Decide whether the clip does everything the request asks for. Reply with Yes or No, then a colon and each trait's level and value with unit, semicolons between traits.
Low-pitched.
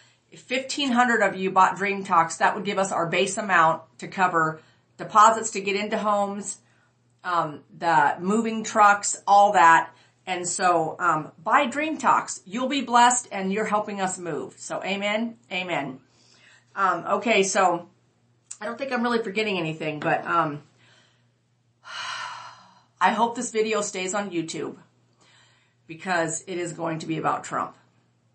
No: medium, 185 Hz